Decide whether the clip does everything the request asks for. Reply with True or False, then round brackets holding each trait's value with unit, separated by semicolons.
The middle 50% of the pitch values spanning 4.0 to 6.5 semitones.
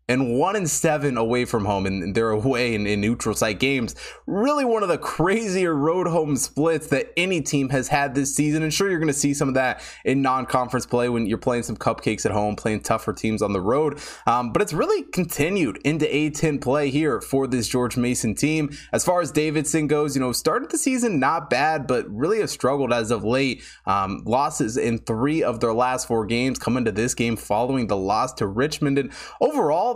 True (4.7 semitones)